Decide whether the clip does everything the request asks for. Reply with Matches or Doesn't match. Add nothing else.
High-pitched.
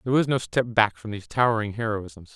Doesn't match